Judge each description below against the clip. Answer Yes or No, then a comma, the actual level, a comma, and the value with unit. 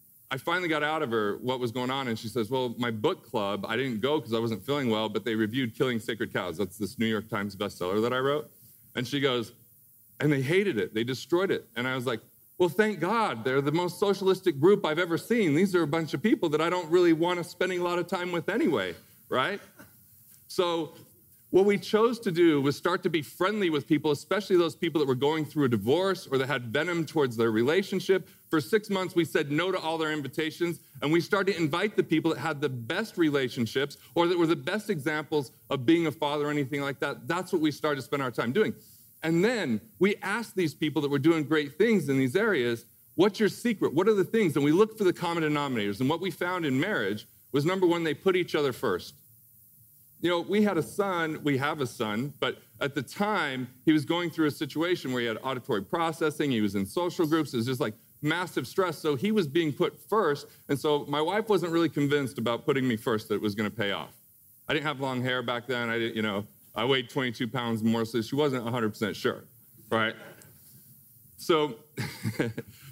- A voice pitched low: No, medium, 150 Hz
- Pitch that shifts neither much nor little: No, wide, 5.8 semitones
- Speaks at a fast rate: Yes, fast, 235 wpm